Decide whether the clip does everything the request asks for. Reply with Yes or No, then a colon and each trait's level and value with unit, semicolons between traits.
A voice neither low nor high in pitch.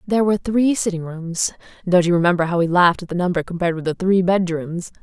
Yes: medium, 180 Hz